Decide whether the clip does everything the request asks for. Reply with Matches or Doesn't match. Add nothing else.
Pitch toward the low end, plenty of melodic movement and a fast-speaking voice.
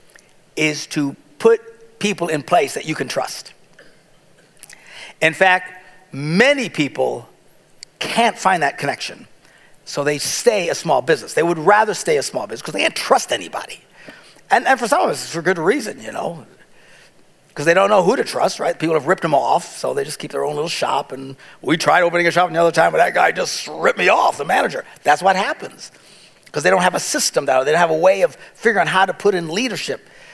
Doesn't match